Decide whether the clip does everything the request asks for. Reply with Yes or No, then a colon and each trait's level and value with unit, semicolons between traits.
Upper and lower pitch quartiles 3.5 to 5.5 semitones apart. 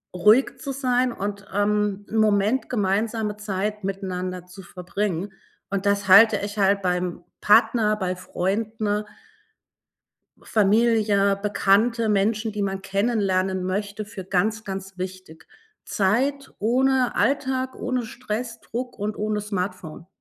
No: narrow, 2.6 semitones